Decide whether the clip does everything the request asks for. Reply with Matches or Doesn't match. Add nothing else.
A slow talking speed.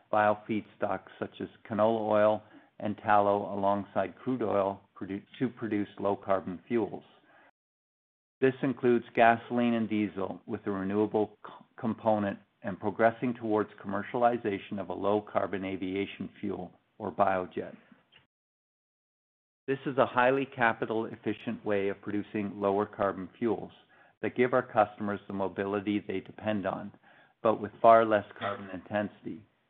Matches